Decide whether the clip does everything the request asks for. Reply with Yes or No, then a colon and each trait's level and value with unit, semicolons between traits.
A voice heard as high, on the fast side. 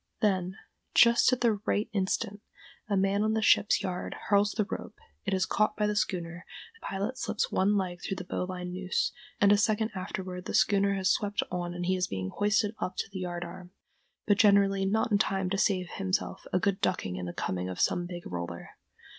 Yes: high, 195 Hz; fast, 210 wpm